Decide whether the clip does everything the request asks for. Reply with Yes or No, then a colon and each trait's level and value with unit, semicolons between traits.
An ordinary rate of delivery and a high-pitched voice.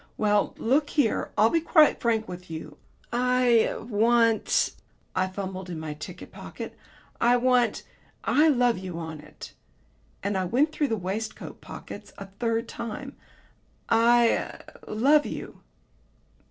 Yes: average, 145 wpm; high, 225 Hz